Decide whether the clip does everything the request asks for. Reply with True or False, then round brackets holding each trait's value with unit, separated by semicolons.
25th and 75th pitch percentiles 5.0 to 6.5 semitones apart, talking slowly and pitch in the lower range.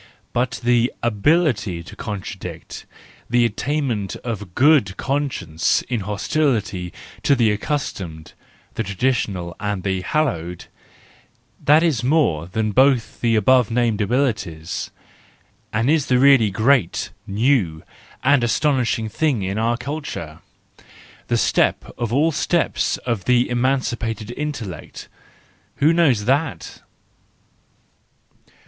True (5.3 semitones; 110 wpm; 120 Hz)